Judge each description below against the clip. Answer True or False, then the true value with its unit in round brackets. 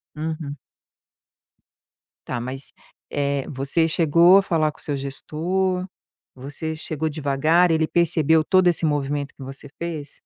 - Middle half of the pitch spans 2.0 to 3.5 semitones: True (3.0 semitones)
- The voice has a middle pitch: True (155 Hz)